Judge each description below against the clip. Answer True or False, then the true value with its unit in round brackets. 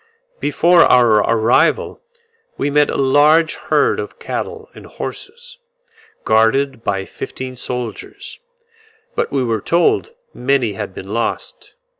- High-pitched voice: False (130 Hz)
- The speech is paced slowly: True (120 wpm)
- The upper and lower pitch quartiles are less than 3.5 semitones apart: False (5.3 semitones)